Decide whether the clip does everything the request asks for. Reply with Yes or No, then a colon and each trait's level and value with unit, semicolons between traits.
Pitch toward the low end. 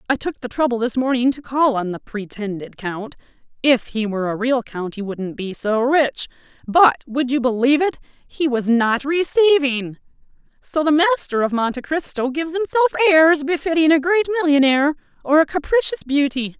No: very high, 275 Hz